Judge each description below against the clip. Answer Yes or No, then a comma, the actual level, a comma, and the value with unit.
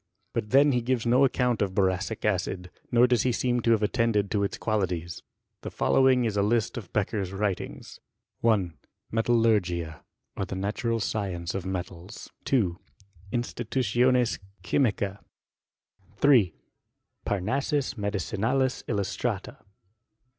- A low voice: Yes, low, 110 Hz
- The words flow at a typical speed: No, slow, 125 wpm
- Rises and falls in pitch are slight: No, average, 4.0 semitones